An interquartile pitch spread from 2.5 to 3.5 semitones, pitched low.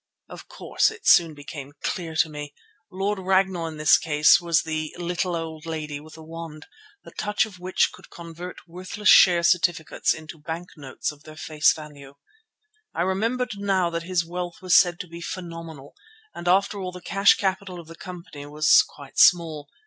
No: average, 2.8 semitones; medium, 170 Hz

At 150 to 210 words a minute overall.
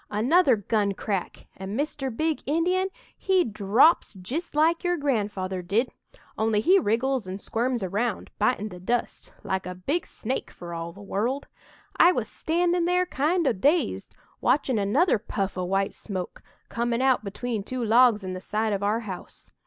Yes: average, 170 wpm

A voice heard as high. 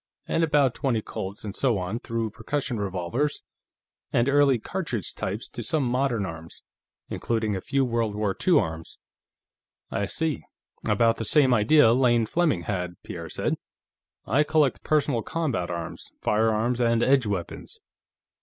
No: low, 115 Hz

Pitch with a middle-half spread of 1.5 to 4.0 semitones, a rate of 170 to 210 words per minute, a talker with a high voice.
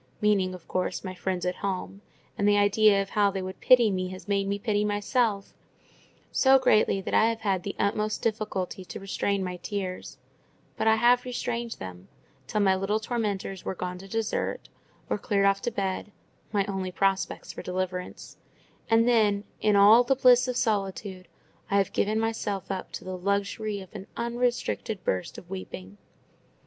Yes: narrow, 2.6 semitones; average, 175 wpm; high, 200 Hz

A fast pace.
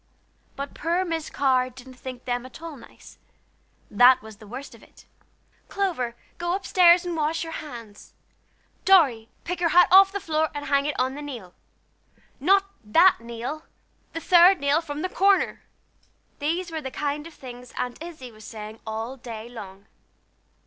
No: average, 170 wpm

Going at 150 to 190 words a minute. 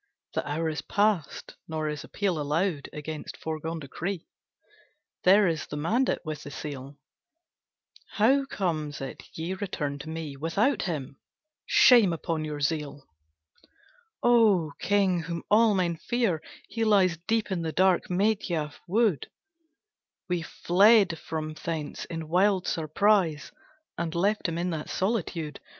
No: slow, 135 wpm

